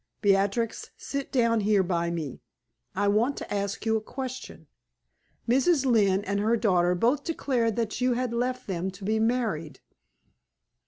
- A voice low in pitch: No, high, 220 Hz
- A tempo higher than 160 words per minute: No, average, 155 wpm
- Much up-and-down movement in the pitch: No, average, 4.0 semitones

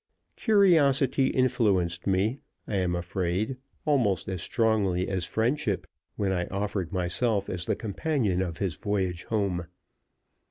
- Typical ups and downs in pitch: Yes, average, 4.8 semitones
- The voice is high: No, low, 100 Hz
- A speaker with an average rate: No, slow, 125 wpm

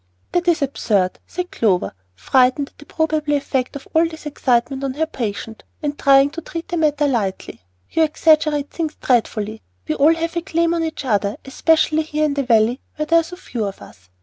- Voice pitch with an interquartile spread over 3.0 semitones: Yes, average, 4.8 semitones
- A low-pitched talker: No, very high, 290 Hz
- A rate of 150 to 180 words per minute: No, average, 200 wpm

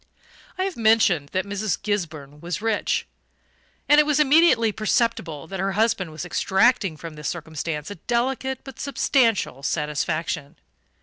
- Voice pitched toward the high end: Yes, high, 195 Hz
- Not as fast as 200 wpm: Yes, average, 140 wpm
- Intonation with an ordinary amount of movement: No, wide, 6.7 semitones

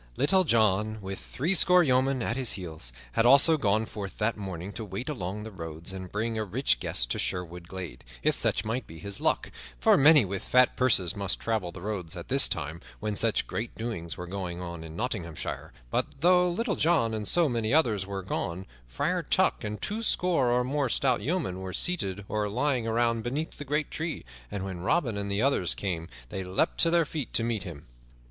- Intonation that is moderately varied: No, wide, 6.0 semitones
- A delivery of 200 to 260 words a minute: Yes, fast, 205 wpm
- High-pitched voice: No, low, 110 Hz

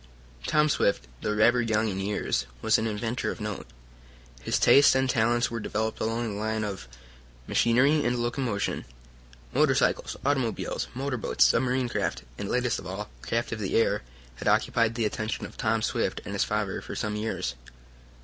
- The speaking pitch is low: Yes, low, 110 Hz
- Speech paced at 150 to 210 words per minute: Yes, average, 170 wpm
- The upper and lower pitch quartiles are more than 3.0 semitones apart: No, narrow, 2.5 semitones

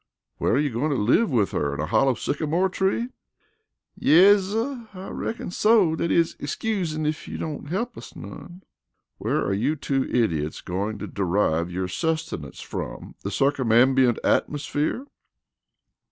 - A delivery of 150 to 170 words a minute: Yes, average, 155 wpm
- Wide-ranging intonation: Yes, wide, 8.8 semitones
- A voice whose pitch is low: No, medium, 145 Hz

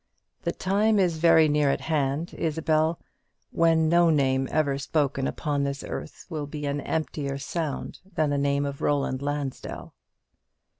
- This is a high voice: No, medium, 150 Hz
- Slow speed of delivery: No, average, 150 wpm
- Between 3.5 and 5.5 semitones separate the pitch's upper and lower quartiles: No, narrow, 2.4 semitones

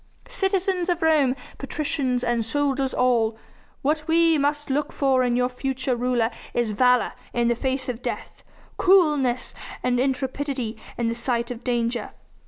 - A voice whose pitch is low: No, very high, 255 Hz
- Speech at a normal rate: Yes, average, 150 wpm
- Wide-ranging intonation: No, average, 3.2 semitones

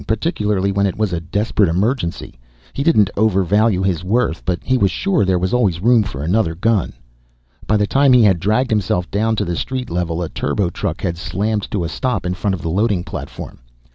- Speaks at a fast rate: Yes, fast, 210 wpm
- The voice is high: No, low, 100 Hz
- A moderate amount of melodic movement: Yes, average, 3.9 semitones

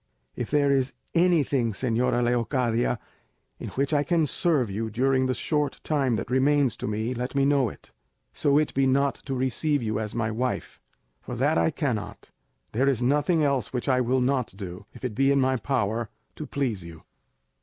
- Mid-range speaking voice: No, low, 130 Hz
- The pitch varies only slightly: No, average, 3.2 semitones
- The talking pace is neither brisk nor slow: Yes, average, 190 wpm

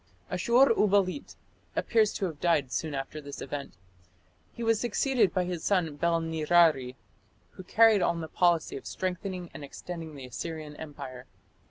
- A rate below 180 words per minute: Yes, average, 155 wpm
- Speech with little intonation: No, average, 4.4 semitones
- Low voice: No, medium, 170 Hz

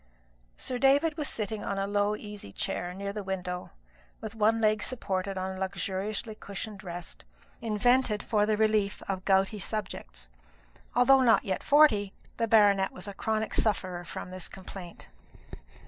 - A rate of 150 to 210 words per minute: Yes, average, 155 wpm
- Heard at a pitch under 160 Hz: No, high, 205 Hz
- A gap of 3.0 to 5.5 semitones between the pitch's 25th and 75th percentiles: No, narrow, 2.5 semitones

